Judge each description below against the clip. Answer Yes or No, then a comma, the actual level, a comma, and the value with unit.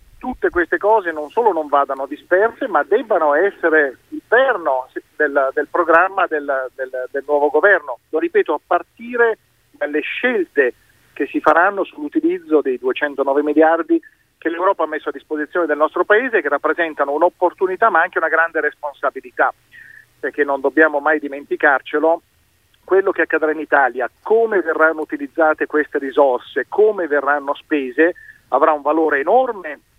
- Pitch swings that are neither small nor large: No, wide, 6.3 semitones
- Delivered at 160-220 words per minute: No, average, 145 wpm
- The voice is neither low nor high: Yes, medium, 160 Hz